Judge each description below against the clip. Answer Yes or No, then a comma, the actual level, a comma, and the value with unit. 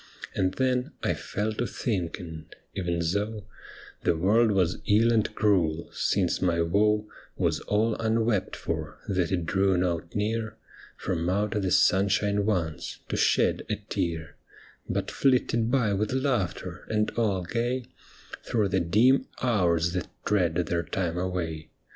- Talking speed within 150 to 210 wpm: No, average, 140 wpm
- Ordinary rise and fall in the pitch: Yes, average, 4.1 semitones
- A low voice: Yes, low, 100 Hz